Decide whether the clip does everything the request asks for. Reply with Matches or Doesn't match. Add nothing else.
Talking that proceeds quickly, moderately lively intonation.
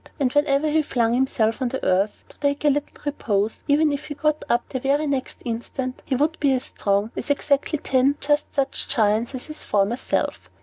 Matches